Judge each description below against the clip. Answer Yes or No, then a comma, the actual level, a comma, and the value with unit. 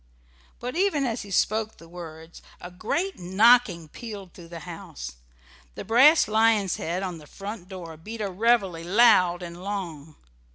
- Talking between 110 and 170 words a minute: Yes, average, 160 wpm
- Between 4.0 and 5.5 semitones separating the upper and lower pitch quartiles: Yes, average, 4.8 semitones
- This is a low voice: No, high, 190 Hz